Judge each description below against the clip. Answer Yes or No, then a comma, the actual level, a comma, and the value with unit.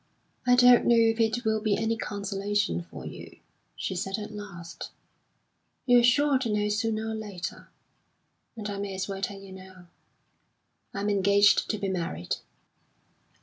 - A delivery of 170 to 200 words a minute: No, average, 155 wpm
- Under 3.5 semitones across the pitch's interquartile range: Yes, narrow, 2.5 semitones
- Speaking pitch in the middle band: No, high, 205 Hz